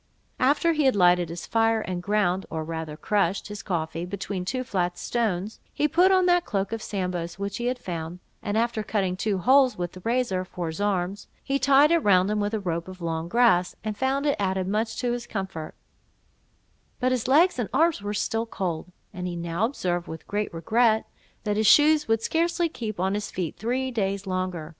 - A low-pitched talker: No, high, 205 Hz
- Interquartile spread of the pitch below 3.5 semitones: No, average, 5.2 semitones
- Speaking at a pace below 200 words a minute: No, fast, 205 wpm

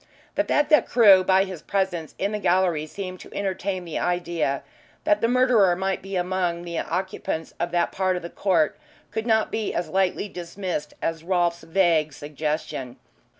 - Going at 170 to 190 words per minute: Yes, average, 180 wpm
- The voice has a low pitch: No, medium, 180 Hz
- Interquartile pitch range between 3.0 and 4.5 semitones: No, narrow, 2.4 semitones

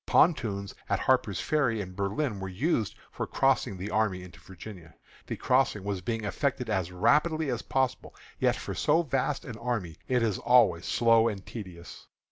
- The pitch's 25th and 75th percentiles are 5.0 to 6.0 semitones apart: Yes, average, 5.3 semitones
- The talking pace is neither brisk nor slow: Yes, average, 170 wpm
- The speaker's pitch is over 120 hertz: No, low, 110 Hz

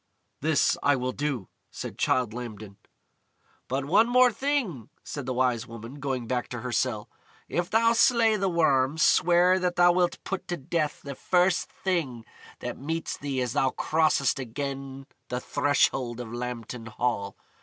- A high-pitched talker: No, low, 135 Hz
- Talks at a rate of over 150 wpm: Yes, average, 160 wpm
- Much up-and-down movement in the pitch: Yes, wide, 5.8 semitones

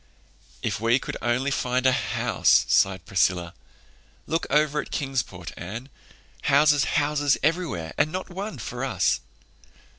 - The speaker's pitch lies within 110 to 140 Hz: Yes, low, 135 Hz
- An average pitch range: No, wide, 6.0 semitones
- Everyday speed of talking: No, slow, 130 wpm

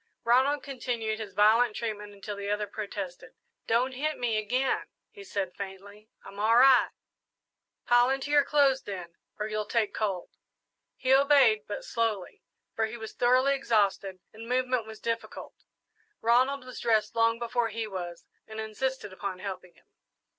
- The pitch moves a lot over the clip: No, average, 3.6 semitones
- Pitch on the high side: Yes, high, 225 Hz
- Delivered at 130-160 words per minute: Yes, average, 155 wpm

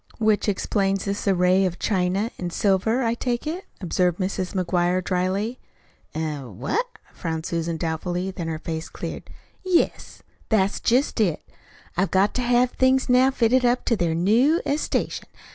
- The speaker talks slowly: No, average, 155 wpm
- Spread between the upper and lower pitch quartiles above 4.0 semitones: Yes, wide, 5.4 semitones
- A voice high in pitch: Yes, high, 195 Hz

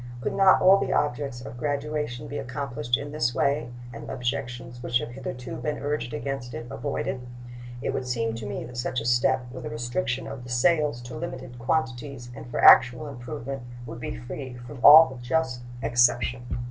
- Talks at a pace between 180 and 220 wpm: Yes, average, 185 wpm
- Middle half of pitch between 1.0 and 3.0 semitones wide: Yes, narrow, 2.6 semitones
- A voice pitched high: No, low, 125 Hz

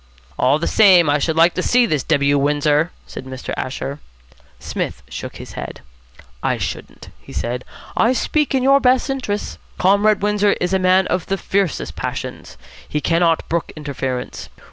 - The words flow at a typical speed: Yes, average, 170 wpm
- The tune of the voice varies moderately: No, wide, 6.0 semitones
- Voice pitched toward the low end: No, medium, 175 Hz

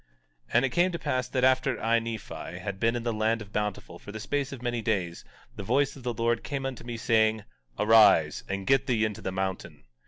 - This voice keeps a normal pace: No, fast, 230 wpm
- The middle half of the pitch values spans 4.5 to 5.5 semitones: No, average, 3.5 semitones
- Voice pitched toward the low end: Yes, low, 115 Hz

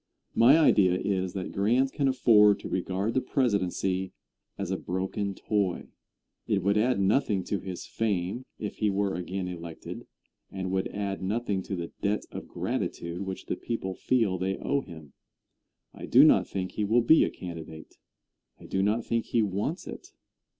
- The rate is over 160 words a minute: Yes, average, 170 wpm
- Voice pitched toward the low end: Yes, low, 100 Hz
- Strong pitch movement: No, average, 3.1 semitones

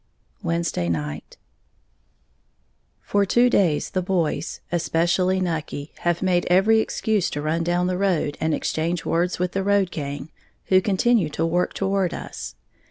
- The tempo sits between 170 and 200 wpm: No, average, 145 wpm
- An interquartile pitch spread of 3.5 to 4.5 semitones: No, average, 2.8 semitones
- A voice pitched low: No, medium, 175 Hz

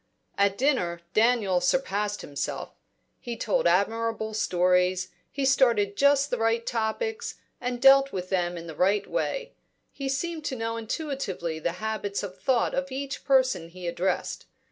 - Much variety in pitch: Yes, wide, 6.4 semitones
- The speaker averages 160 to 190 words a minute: No, average, 150 wpm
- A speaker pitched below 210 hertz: No, high, 220 Hz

